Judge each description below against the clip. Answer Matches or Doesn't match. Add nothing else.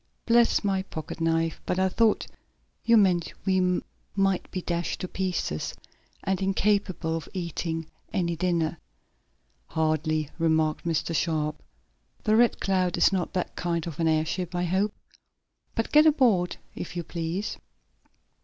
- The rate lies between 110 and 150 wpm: Matches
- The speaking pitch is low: Doesn't match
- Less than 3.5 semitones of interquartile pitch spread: Matches